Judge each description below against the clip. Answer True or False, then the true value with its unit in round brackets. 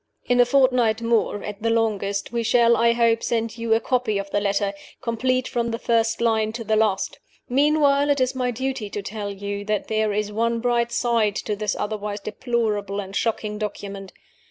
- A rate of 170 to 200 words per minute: True (195 wpm)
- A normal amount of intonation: False (2.3 semitones)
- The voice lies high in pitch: True (225 Hz)